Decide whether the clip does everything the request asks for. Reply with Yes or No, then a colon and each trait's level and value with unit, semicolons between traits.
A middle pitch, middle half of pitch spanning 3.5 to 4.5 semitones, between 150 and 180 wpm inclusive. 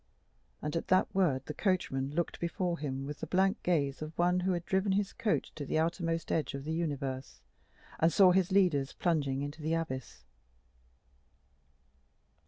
Yes: medium, 165 Hz; average, 4.2 semitones; average, 170 wpm